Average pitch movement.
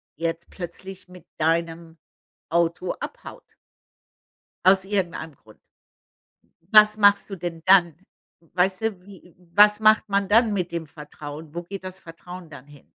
Yes: average, 3.2 semitones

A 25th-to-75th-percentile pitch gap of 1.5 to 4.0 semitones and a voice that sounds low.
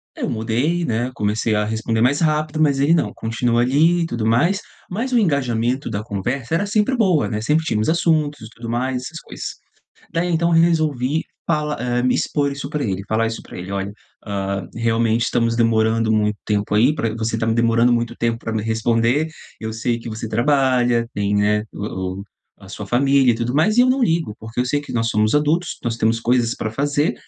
No: average, 5.0 semitones; low, 120 Hz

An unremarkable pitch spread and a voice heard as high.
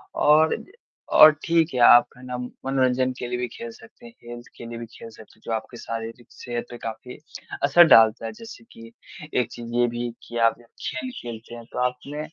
No: average, 3.8 semitones; low, 125 Hz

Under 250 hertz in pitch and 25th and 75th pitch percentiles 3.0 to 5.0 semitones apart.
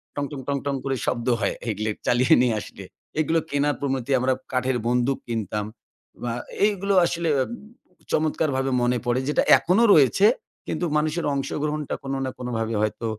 Yes: low, 135 Hz; average, 3.7 semitones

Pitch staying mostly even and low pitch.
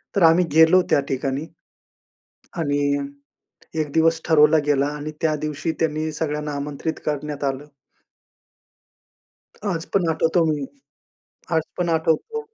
No: narrow, 1.9 semitones; medium, 155 Hz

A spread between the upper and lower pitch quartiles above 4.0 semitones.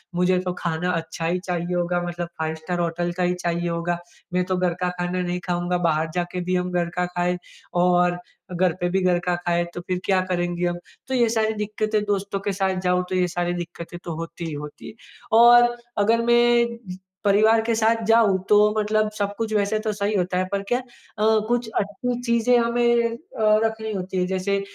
No: average, 3.6 semitones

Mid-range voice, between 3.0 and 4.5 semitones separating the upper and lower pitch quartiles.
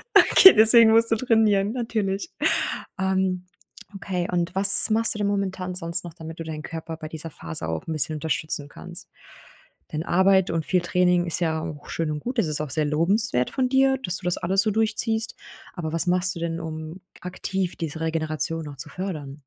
Yes: medium, 180 Hz; average, 3.8 semitones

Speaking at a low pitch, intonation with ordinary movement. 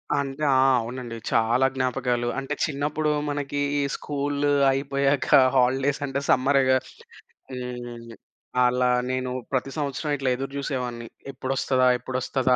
No: low, 130 Hz; narrow, 1.9 semitones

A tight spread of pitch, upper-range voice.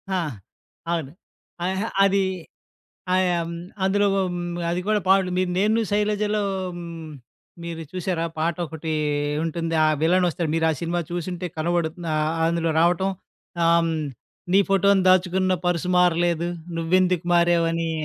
No: narrow, 2.1 semitones; medium, 175 Hz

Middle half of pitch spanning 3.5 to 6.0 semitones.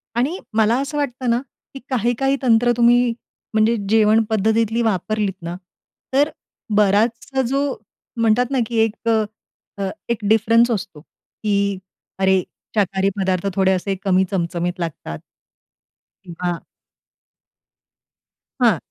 Yes: average, 3.8 semitones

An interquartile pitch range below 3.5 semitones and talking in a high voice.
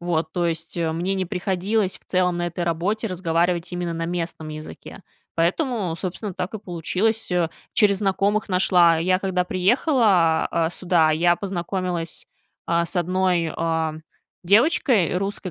No: narrow, 2.5 semitones; medium, 180 Hz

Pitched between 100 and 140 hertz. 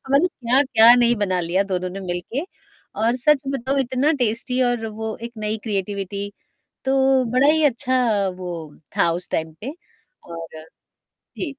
No: high, 235 Hz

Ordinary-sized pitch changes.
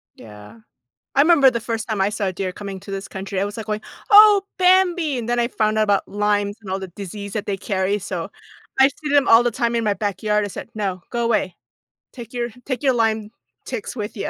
Yes: average, 3.3 semitones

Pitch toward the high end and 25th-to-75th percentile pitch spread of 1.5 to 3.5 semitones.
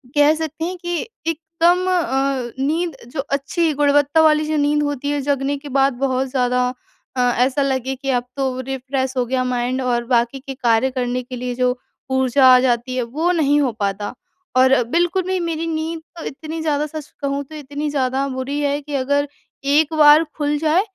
Yes: very high, 280 Hz; average, 3.2 semitones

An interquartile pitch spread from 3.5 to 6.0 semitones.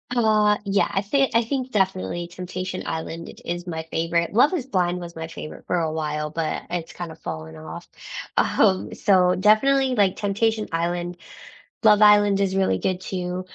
Yes: average, 3.9 semitones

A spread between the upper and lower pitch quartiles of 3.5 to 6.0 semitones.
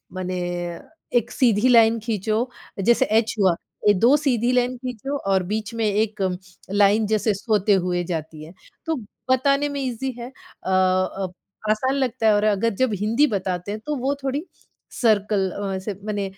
Yes: average, 4.0 semitones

